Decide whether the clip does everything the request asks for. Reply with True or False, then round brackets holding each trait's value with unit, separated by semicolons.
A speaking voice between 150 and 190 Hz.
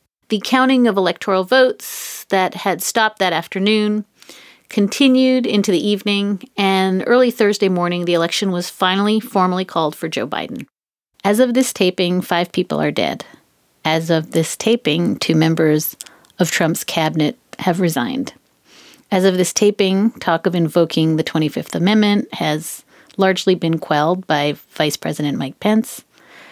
True (185 Hz)